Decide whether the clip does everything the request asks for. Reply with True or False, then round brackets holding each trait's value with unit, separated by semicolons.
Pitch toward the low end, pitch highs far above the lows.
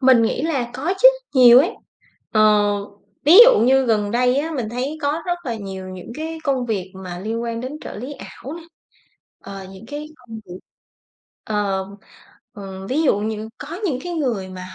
False (235 Hz; 5.7 semitones)